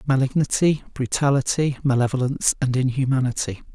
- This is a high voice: No, low, 135 Hz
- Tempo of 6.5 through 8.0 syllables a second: No, 5.7 syllables/s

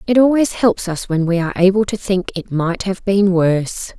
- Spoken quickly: Yes, fast, 225 wpm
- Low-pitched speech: No, high, 190 Hz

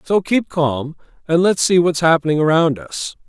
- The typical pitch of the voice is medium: Yes, medium, 165 Hz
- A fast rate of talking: No, average, 185 wpm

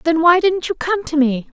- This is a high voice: Yes, very high, 325 Hz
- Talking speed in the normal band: No, fast, 265 wpm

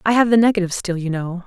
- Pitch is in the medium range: No, high, 195 Hz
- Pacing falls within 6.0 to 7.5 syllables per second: Yes, 7.3 syllables/s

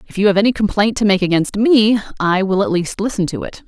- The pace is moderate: No, fast, 245 wpm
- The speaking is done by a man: No, female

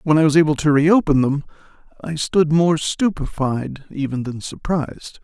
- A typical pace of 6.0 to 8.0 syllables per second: No, 4.7 syllables/s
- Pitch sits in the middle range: Yes, medium, 155 Hz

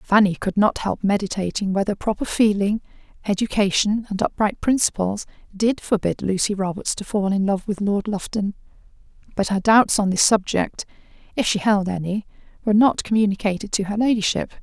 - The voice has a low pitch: No, high, 205 Hz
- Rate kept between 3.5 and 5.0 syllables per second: No, 5.4 syllables/s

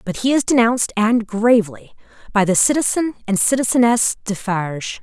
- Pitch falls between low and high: No, high, 220 Hz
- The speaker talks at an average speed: No, slow, 120 wpm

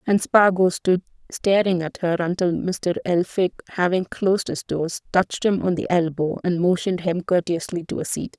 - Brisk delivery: No, average, 180 wpm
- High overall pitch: No, medium, 180 Hz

